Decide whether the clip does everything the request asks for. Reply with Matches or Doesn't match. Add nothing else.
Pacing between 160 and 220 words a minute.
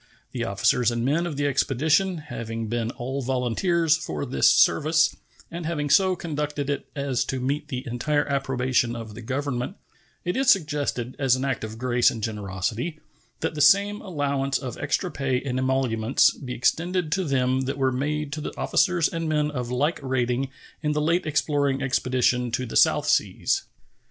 Matches